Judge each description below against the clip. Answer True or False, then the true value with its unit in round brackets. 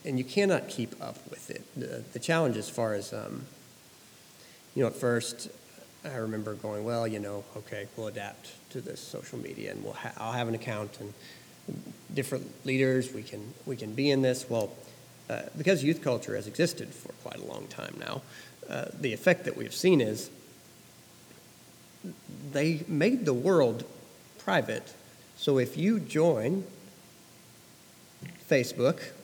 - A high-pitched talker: False (125 Hz)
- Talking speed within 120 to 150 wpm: False (160 wpm)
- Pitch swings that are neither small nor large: False (5.8 semitones)